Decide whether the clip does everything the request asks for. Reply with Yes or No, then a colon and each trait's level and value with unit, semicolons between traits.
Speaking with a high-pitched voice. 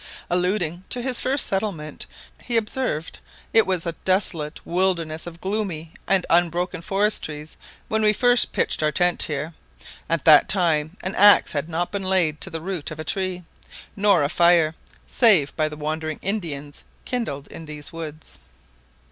No: medium, 175 Hz